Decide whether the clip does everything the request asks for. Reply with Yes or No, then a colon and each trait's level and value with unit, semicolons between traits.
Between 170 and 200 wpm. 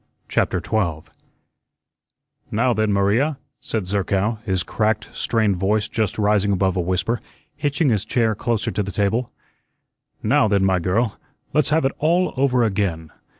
No: average, 150 wpm